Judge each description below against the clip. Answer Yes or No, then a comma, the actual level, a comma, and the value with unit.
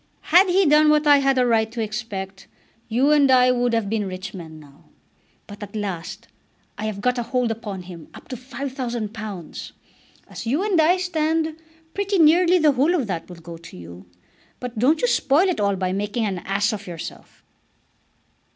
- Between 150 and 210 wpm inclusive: Yes, average, 190 wpm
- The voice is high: Yes, high, 230 Hz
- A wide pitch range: Yes, wide, 7.0 semitones